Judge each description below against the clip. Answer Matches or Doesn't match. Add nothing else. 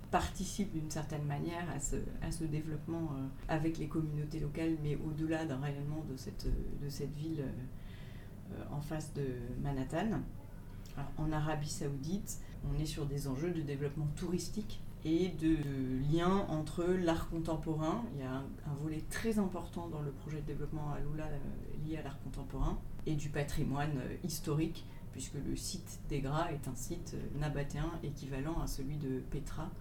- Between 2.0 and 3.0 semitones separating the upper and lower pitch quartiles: Matches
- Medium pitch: Matches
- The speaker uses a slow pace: Doesn't match